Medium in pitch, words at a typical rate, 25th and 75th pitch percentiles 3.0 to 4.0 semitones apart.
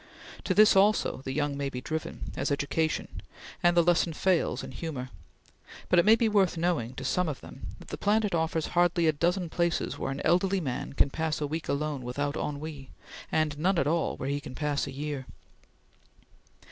Yes: medium, 155 Hz; average, 195 wpm; average, 3.6 semitones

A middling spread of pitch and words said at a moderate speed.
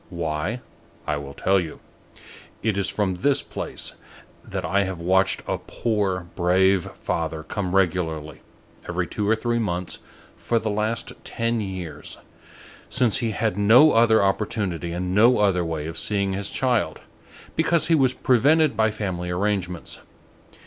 Yes: average, 4.1 semitones; average, 150 wpm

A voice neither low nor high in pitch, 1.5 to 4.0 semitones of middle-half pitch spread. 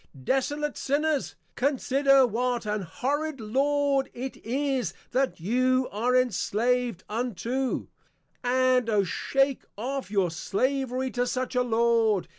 No: very high, 255 Hz; average, 2.9 semitones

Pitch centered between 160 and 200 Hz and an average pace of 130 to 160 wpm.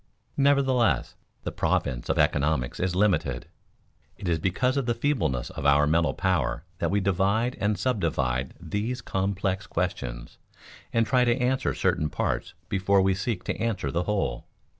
No: very low, 95 Hz; average, 155 wpm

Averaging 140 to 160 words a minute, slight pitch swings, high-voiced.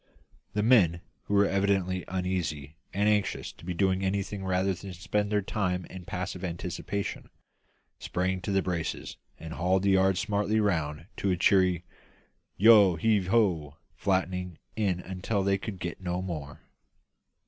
No: average, 150 wpm; narrow, 2.1 semitones; very low, 95 Hz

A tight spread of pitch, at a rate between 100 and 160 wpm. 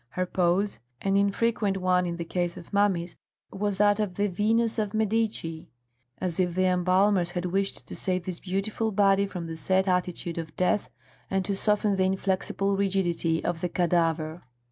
No: narrow, 2.3 semitones; average, 175 wpm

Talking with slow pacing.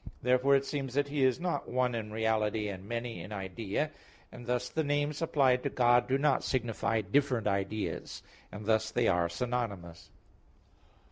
No: average, 165 wpm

